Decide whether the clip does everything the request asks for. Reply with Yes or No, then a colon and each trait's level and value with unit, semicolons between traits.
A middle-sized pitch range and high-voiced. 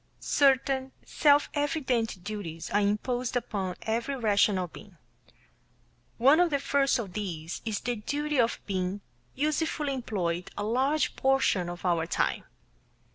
No: wide, 6.1 semitones; high, 230 Hz